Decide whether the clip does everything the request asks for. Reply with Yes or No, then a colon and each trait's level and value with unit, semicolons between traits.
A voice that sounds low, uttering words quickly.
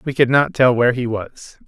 Yes: low, 125 Hz; fast, 250 wpm